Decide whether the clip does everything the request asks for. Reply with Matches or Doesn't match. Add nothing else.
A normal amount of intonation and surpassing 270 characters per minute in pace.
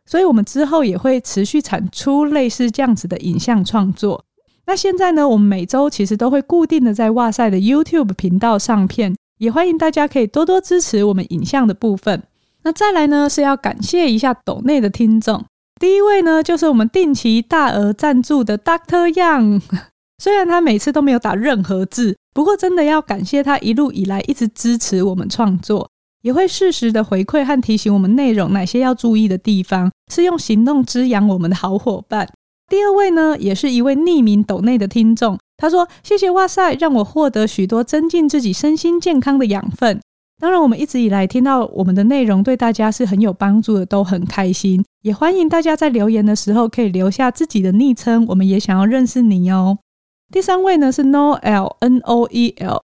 Doesn't match